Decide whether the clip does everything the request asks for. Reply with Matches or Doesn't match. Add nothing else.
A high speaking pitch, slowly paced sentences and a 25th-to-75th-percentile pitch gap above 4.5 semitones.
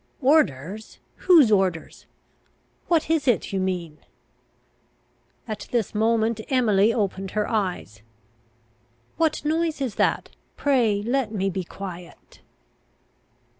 Matches